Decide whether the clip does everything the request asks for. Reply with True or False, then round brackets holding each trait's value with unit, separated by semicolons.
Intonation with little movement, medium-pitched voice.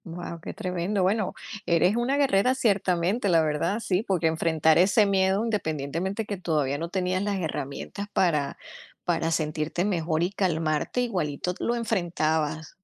False (3.9 semitones; 180 Hz)